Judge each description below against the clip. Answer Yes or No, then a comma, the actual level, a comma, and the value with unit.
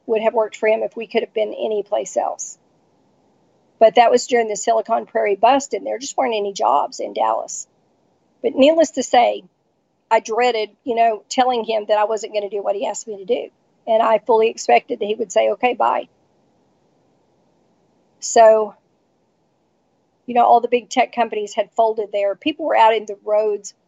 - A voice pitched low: No, high, 225 Hz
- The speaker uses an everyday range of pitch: No, narrow, 2.2 semitones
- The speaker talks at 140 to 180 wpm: No, average, 195 wpm